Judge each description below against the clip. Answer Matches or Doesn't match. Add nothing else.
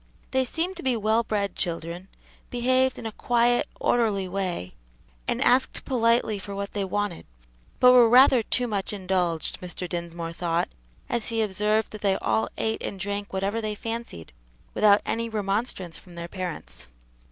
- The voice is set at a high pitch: Matches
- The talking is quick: Doesn't match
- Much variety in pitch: Doesn't match